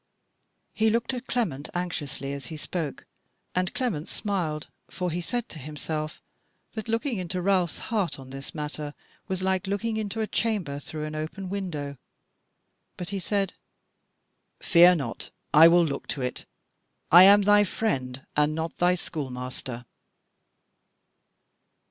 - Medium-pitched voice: Yes, medium, 175 Hz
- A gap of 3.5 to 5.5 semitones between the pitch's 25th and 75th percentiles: Yes, average, 5.2 semitones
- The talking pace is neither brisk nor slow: Yes, average, 145 wpm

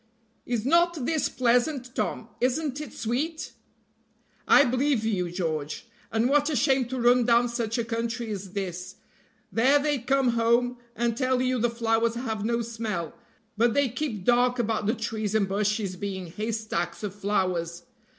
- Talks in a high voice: Yes, high, 235 Hz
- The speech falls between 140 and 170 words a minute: Yes, average, 160 wpm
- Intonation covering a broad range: No, average, 3.2 semitones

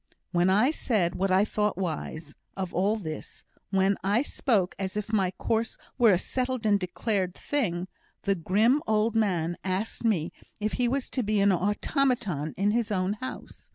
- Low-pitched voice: No, high, 200 Hz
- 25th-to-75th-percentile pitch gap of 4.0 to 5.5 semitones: No, average, 3.4 semitones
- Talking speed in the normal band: Yes, average, 175 wpm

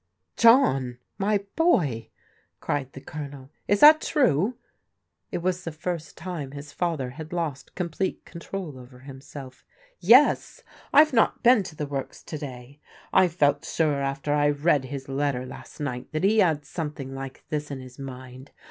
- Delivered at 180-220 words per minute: No, average, 170 wpm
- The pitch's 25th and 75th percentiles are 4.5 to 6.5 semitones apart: Yes, average, 4.9 semitones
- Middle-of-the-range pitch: Yes, medium, 145 Hz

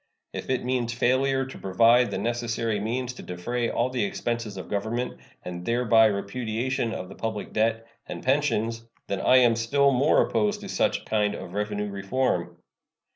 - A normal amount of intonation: Yes, average, 3.3 semitones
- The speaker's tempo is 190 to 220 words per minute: No, average, 170 wpm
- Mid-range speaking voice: No, low, 115 Hz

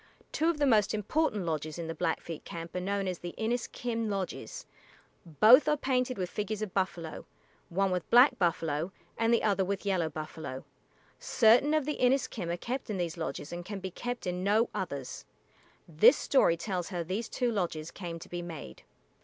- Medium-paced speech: Yes, average, 185 wpm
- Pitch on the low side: No, high, 190 Hz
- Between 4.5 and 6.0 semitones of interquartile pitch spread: Yes, wide, 5.4 semitones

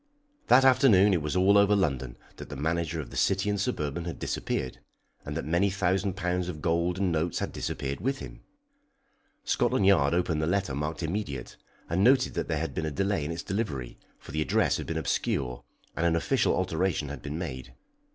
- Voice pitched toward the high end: No, very low, 85 Hz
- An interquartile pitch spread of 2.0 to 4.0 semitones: No, average, 4.4 semitones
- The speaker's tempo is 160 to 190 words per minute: No, average, 200 wpm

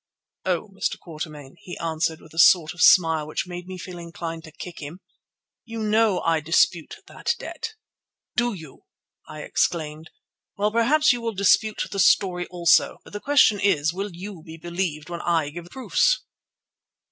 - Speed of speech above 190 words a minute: No, average, 170 wpm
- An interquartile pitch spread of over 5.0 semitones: No, average, 3.9 semitones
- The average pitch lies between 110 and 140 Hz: No, medium, 175 Hz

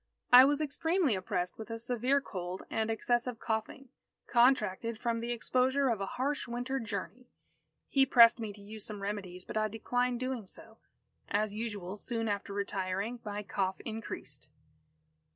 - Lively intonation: No, average, 3.4 semitones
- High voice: Yes, high, 225 Hz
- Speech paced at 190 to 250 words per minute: No, average, 155 wpm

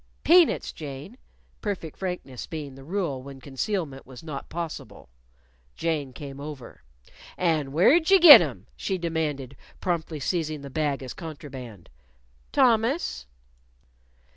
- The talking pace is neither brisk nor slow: No, slow, 120 wpm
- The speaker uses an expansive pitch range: No, average, 4.7 semitones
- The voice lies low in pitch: No, medium, 155 Hz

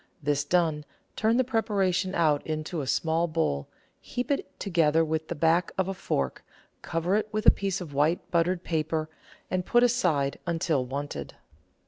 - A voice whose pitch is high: No, medium, 165 Hz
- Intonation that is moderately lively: Yes, average, 3.6 semitones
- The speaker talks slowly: No, average, 165 wpm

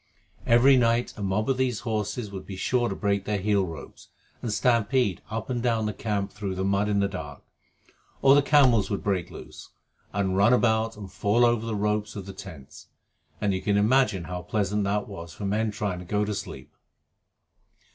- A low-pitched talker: Yes, low, 105 Hz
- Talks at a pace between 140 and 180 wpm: No, average, 200 wpm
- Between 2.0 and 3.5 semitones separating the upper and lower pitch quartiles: Yes, average, 2.8 semitones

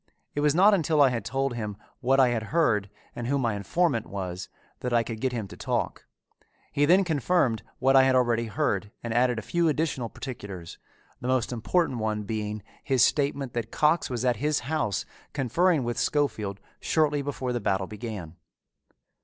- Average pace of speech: Yes, average, 185 wpm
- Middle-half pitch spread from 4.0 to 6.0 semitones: Yes, average, 4.8 semitones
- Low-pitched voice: Yes, low, 125 Hz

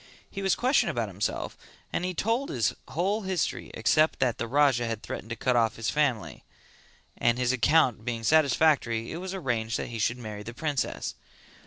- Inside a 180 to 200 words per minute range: Yes, average, 185 wpm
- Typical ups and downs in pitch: No, wide, 5.9 semitones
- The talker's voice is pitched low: Yes, low, 130 Hz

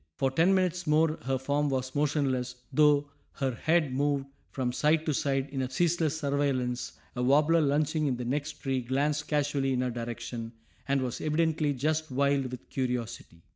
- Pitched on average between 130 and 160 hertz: Yes, medium, 140 Hz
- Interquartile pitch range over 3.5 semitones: No, average, 2.9 semitones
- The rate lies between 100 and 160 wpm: No, average, 175 wpm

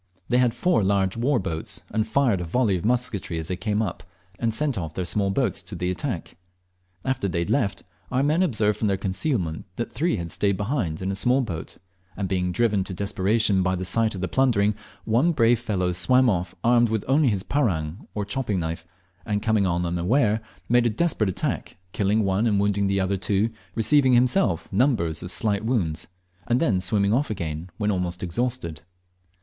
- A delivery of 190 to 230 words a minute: Yes, average, 200 wpm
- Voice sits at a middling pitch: No, low, 105 Hz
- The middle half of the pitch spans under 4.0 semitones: No, average, 4.5 semitones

